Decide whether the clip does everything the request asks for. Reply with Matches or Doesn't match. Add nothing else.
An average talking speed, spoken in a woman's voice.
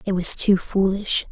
Matches